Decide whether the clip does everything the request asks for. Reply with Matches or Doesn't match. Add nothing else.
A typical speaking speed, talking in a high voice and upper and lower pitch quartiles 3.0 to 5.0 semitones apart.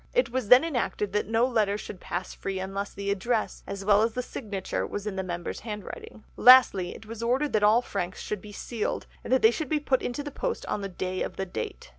Doesn't match